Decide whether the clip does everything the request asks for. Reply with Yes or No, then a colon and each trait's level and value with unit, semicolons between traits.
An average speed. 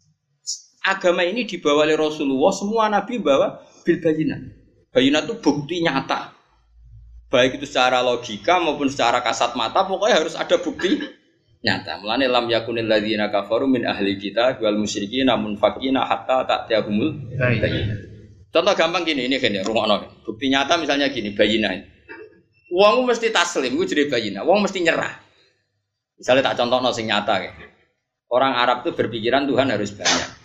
No: fast, 150 wpm